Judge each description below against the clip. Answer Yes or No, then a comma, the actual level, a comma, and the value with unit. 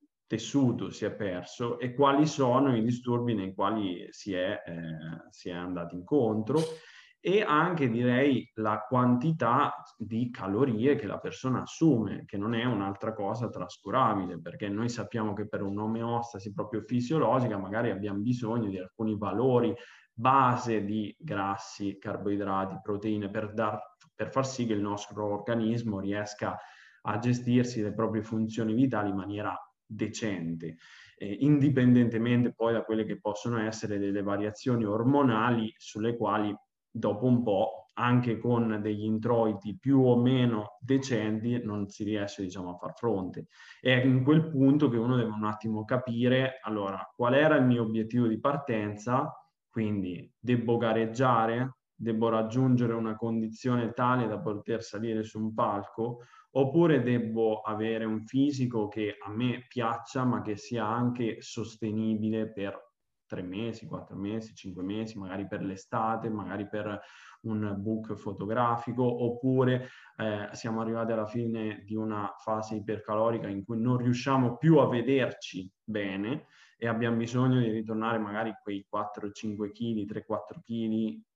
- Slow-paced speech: No, average, 140 wpm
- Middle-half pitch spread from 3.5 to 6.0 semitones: No, average, 2.8 semitones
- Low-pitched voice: Yes, low, 110 Hz